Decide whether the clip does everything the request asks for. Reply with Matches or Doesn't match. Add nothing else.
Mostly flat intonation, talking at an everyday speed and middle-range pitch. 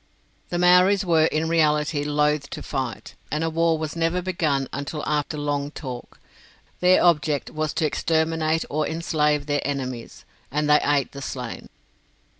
Matches